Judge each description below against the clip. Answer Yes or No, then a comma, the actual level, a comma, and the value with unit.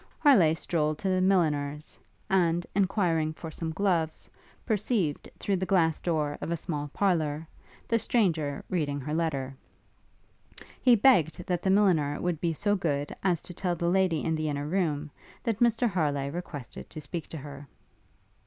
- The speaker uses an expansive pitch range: No, average, 4.0 semitones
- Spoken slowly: No, average, 165 wpm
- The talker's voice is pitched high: No, medium, 165 Hz